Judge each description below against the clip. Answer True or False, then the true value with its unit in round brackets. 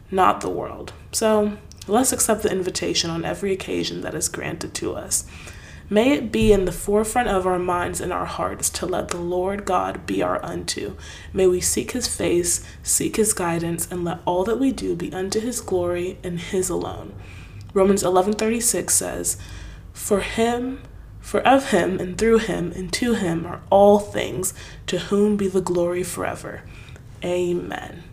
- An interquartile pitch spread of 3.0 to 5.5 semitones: True (3.7 semitones)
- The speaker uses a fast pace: False (175 wpm)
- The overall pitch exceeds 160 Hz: True (185 Hz)